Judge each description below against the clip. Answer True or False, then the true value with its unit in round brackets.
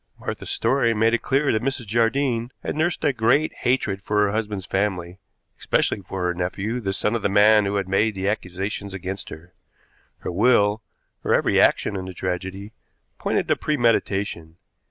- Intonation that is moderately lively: True (3.4 semitones)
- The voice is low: True (105 Hz)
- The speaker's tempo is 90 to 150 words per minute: False (175 wpm)